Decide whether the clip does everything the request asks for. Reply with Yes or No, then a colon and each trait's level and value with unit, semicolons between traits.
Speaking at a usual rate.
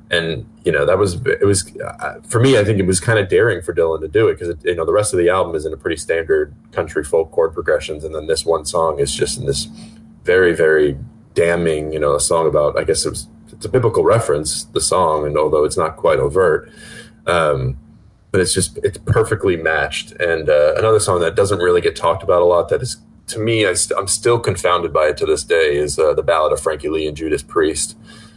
No: fast, 240 wpm